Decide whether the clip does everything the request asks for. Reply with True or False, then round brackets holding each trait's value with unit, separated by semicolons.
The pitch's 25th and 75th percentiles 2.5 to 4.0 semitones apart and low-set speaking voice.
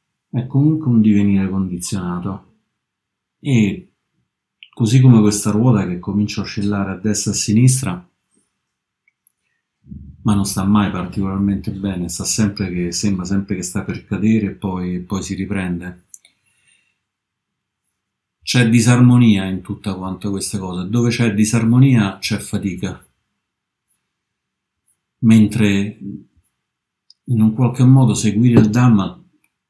True (2.9 semitones; 105 Hz)